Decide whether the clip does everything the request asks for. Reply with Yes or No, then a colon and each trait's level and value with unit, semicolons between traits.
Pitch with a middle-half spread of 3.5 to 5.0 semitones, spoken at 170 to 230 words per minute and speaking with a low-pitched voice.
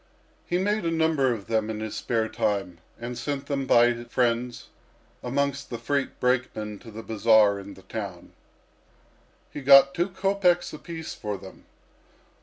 No: average, 4.5 semitones; average, 160 wpm; low, 120 Hz